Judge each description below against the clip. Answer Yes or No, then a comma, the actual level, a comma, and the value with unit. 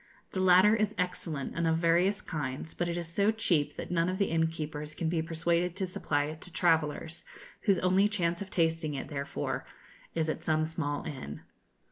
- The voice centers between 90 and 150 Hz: No, medium, 165 Hz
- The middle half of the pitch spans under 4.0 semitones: Yes, narrow, 2.6 semitones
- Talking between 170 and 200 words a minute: Yes, average, 190 wpm